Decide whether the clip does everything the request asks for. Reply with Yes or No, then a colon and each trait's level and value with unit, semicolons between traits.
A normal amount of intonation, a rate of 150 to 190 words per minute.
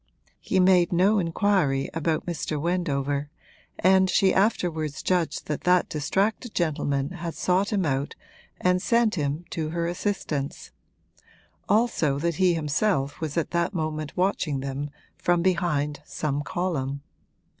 No: average, 4.1 semitones; slow, 135 wpm